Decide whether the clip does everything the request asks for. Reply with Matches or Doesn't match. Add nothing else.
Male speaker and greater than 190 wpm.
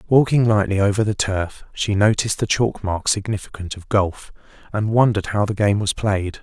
Doesn't match